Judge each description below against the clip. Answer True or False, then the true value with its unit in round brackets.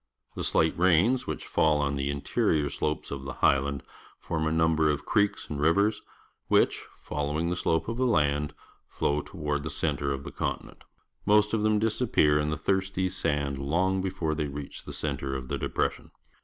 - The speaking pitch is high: False (80 Hz)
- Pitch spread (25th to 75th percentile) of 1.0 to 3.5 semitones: False (4.6 semitones)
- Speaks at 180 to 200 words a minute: True (185 wpm)